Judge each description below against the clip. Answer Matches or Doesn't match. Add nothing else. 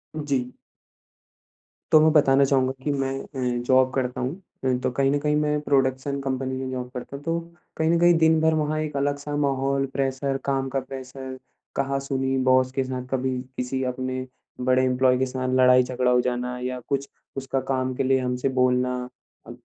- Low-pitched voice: Matches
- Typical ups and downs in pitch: Doesn't match